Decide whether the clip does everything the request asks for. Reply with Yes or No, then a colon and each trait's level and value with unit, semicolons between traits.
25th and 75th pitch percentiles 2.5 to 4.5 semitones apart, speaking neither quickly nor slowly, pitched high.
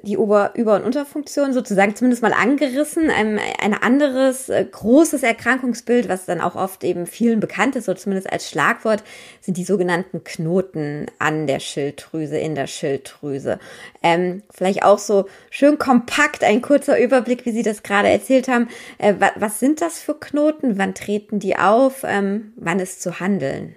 No: wide, 5.4 semitones; average, 170 wpm; high, 210 Hz